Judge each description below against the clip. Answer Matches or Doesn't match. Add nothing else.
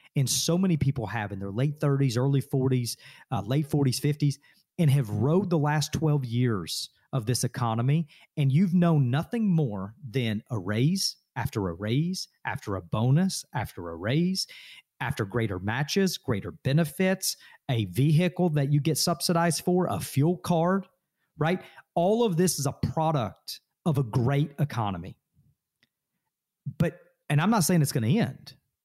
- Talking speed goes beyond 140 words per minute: Matches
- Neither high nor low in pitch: Matches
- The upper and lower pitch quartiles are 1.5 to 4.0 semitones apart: Doesn't match